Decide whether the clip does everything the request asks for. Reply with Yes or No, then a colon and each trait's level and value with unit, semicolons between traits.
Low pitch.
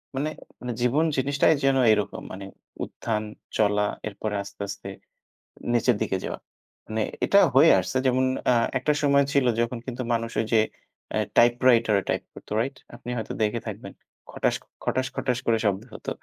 Yes: low, 120 Hz